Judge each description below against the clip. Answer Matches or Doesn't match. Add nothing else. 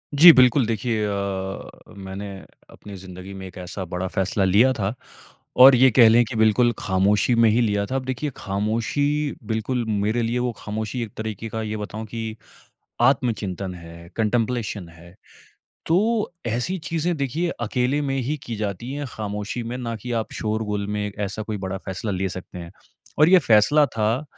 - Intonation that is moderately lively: Matches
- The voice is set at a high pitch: Doesn't match